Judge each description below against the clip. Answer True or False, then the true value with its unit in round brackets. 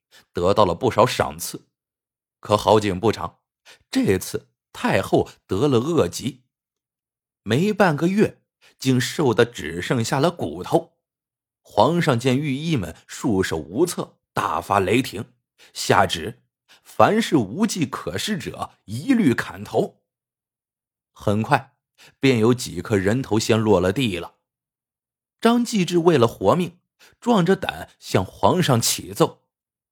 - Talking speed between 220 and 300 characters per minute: False (175 characters per minute)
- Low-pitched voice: True (130 Hz)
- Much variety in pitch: True (7.5 semitones)